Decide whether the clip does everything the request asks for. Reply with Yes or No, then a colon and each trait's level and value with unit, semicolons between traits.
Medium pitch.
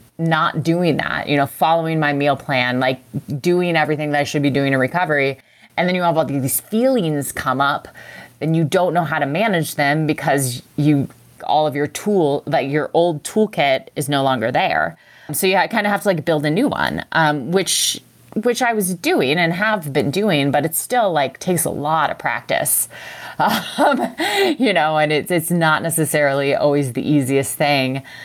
Yes: medium, 155 Hz